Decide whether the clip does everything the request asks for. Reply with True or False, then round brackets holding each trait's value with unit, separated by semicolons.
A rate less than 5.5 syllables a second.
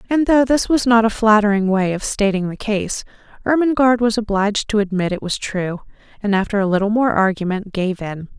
False (5.6 syllables/s)